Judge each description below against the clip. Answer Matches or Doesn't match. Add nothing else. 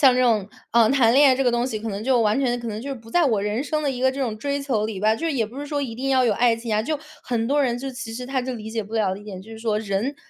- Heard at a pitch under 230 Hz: Doesn't match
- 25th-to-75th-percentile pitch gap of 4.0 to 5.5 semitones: Doesn't match